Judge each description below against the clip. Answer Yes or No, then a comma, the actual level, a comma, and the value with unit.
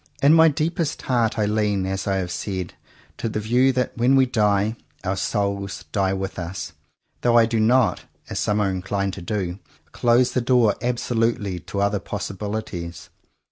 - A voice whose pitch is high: No, low, 105 Hz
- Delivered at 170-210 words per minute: Yes, average, 175 wpm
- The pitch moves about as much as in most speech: Yes, average, 3.7 semitones